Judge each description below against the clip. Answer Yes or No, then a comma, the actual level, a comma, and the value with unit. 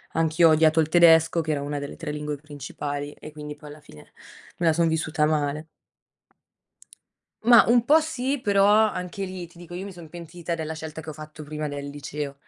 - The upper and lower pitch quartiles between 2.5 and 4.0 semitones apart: Yes, average, 2.8 semitones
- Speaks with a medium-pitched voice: Yes, medium, 160 Hz